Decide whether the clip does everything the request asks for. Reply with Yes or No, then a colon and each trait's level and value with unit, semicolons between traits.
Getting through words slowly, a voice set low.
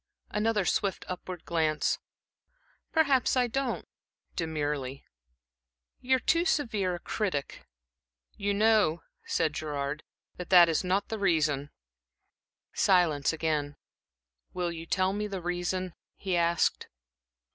No: slow, 115 wpm; medium, 180 Hz